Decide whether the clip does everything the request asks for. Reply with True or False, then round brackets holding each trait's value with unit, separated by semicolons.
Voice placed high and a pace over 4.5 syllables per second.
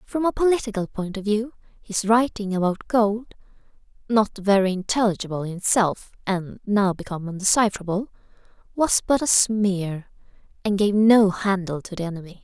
True (205 Hz; 5.2 syllables/s)